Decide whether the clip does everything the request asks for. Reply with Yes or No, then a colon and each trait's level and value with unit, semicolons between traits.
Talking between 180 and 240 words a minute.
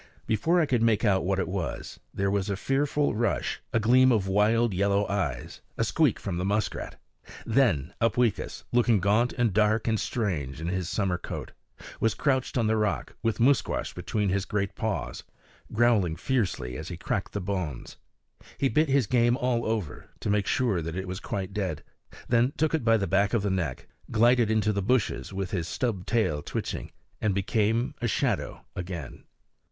Yes: average, 185 wpm